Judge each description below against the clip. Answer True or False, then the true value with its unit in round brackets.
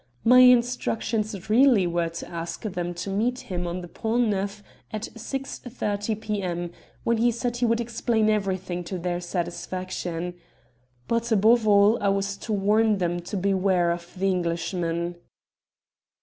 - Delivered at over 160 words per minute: False (150 wpm)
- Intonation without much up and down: False (4.2 semitones)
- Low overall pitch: False (200 Hz)